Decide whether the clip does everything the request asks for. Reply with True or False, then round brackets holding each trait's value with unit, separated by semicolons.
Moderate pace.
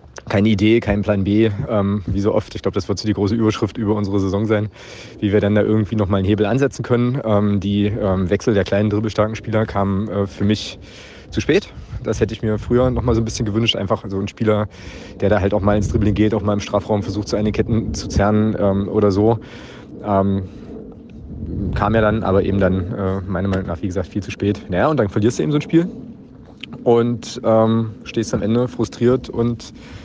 False (225 wpm)